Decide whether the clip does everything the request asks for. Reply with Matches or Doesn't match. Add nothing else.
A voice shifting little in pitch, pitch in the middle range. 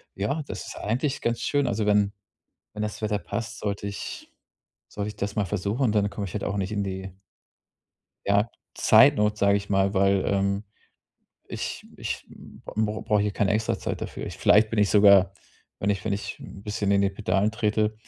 Doesn't match